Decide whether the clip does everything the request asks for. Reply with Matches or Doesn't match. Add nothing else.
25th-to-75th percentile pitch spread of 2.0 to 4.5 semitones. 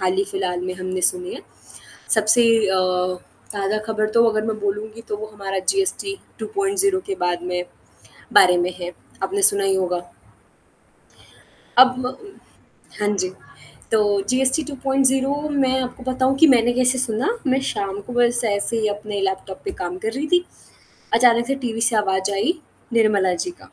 Doesn't match